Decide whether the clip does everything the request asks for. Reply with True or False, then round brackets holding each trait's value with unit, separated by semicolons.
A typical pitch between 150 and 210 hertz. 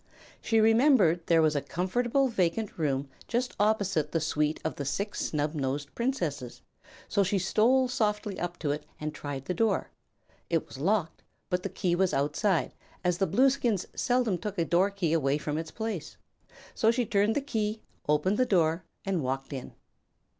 True (185 Hz)